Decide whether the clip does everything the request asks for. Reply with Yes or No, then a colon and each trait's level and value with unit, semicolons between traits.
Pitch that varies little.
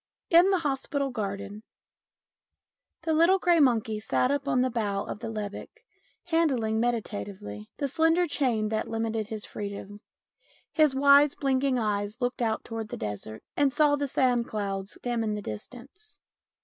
No: average, 5.1 semitones